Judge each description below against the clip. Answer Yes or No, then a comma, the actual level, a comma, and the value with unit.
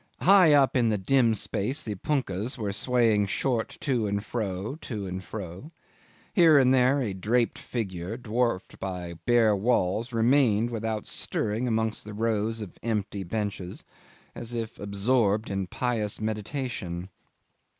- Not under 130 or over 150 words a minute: Yes, average, 145 wpm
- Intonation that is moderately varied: Yes, average, 3.6 semitones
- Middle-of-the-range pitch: No, low, 110 Hz